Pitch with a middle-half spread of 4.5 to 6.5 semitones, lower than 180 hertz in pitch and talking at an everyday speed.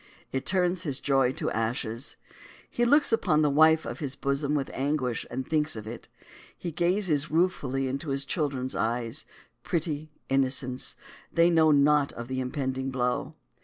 No: average, 3.4 semitones; medium, 140 Hz; average, 165 wpm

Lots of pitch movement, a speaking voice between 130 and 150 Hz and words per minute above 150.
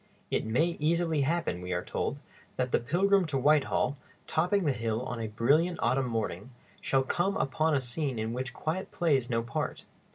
Yes: wide, 5.7 semitones; low, 135 Hz; average, 185 wpm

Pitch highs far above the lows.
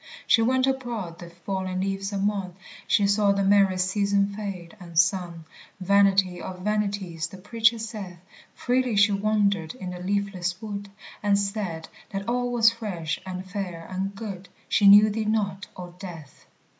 No: narrow, 2.4 semitones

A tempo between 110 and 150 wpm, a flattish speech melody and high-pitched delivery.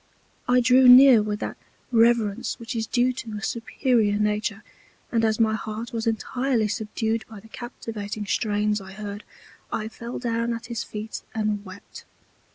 No: average, 165 wpm; narrow, 2.0 semitones; high, 225 Hz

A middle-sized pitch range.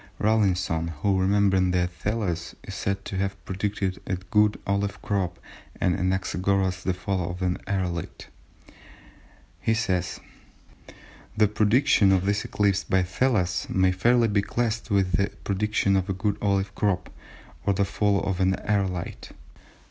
No: narrow, 1.8 semitones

